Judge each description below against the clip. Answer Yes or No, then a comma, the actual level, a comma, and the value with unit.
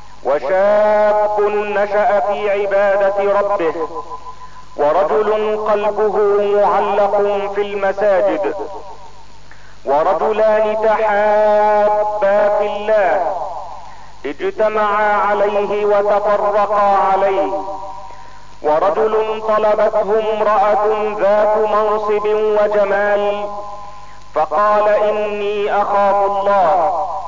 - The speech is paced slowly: Yes, slow, 60 wpm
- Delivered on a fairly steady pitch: Yes, narrow, 0.8 semitones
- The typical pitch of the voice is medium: No, high, 205 Hz